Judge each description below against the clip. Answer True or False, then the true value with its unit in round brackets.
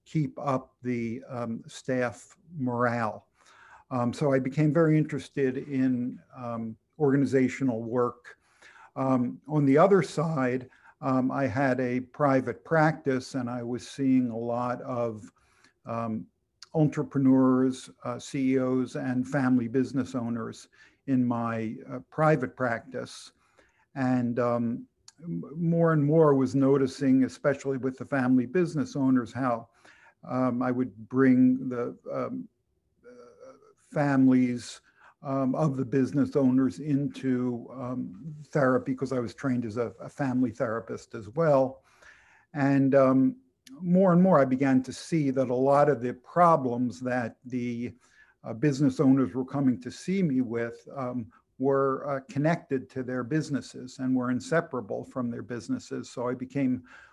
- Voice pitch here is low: True (130 Hz)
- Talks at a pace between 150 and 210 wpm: False (135 wpm)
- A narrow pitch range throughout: True (2.0 semitones)